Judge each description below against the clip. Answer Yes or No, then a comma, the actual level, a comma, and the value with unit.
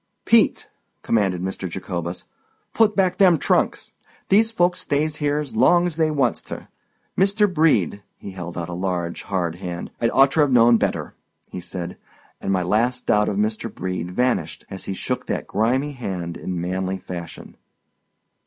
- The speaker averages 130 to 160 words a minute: Yes, average, 150 wpm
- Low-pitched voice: Yes, low, 105 Hz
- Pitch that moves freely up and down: Yes, wide, 8.5 semitones